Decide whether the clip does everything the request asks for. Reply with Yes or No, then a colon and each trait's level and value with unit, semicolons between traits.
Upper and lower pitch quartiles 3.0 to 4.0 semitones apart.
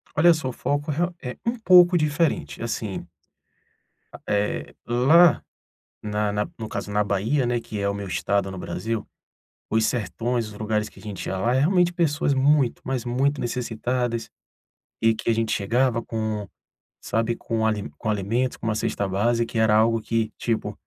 Yes: average, 3.7 semitones